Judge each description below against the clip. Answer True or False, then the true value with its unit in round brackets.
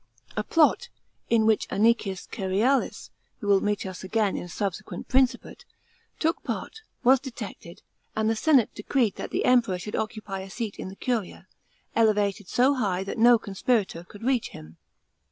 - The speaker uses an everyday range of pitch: True (4.0 semitones)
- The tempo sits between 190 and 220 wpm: False (165 wpm)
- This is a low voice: False (215 Hz)